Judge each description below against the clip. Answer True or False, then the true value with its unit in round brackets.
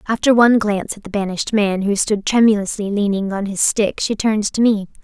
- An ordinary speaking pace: False (215 wpm)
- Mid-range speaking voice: False (205 Hz)